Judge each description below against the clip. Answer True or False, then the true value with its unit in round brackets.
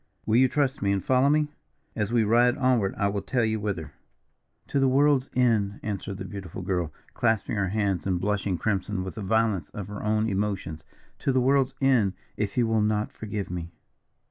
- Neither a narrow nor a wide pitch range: True (3.9 semitones)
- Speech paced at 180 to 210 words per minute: True (195 wpm)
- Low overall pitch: True (105 Hz)